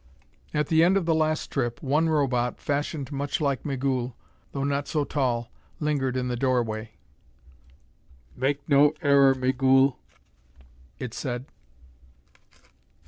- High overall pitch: No, low, 135 Hz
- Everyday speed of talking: No, slow, 125 wpm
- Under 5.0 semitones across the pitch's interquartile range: Yes, narrow, 2.5 semitones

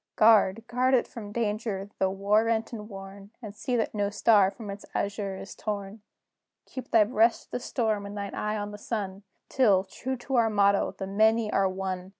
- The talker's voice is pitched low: No, high, 210 Hz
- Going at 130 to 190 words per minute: No, average, 200 wpm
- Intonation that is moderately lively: No, narrow, 2.3 semitones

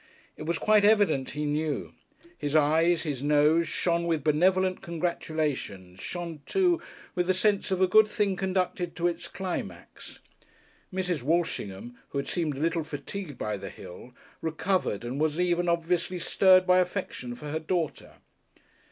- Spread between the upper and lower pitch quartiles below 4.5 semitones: Yes, average, 3.7 semitones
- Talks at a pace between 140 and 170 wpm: Yes, average, 155 wpm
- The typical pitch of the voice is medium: Yes, medium, 170 Hz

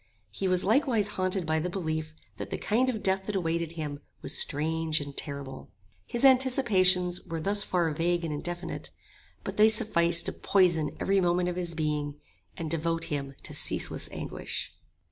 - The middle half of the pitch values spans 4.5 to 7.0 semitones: No, average, 3.5 semitones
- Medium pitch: Yes, medium, 175 Hz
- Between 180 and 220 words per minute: No, average, 170 wpm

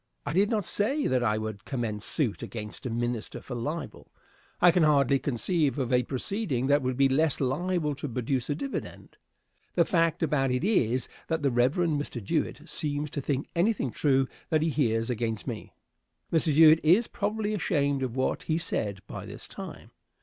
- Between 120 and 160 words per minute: No, average, 185 wpm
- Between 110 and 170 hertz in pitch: Yes, medium, 140 Hz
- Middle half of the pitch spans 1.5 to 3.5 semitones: No, average, 4.9 semitones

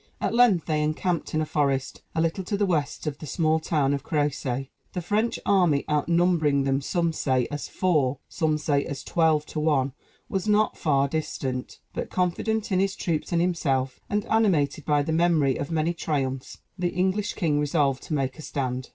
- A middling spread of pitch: Yes, average, 3.8 semitones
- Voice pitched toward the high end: No, medium, 155 Hz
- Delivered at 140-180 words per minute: No, average, 190 wpm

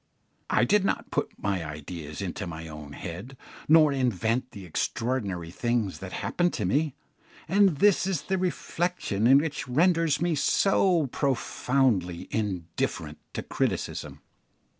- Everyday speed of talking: No, slow, 130 wpm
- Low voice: Yes, low, 125 Hz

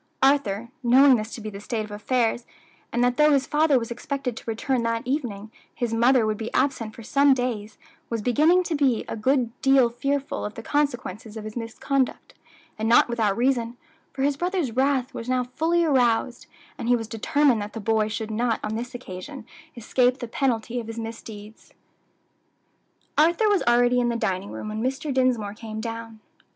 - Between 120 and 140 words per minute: No, average, 190 wpm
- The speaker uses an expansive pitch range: No, average, 3.3 semitones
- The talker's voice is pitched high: Yes, high, 240 Hz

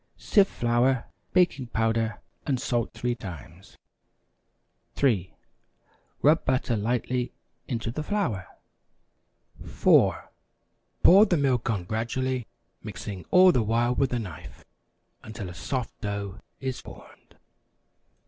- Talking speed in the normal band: No, slow, 110 wpm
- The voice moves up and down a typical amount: Yes, average, 3.8 semitones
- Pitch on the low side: Yes, low, 120 Hz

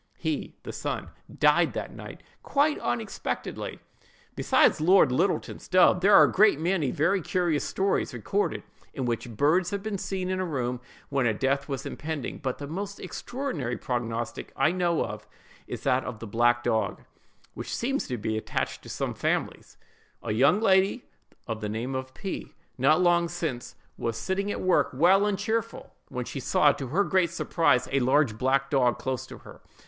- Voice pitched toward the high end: No, medium, 145 Hz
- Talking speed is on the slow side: No, average, 175 wpm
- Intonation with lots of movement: Yes, wide, 7.1 semitones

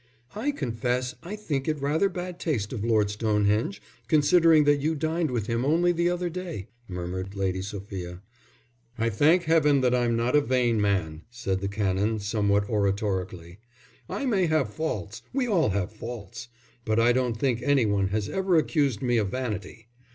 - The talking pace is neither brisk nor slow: Yes, average, 175 wpm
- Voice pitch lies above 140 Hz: No, low, 120 Hz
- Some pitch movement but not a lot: No, wide, 7.2 semitones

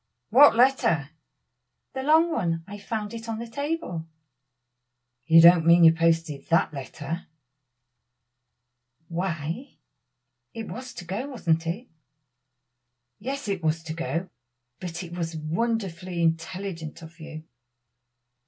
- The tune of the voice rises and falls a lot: Yes, wide, 5.7 semitones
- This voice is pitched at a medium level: Yes, medium, 175 Hz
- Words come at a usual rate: No, slow, 120 wpm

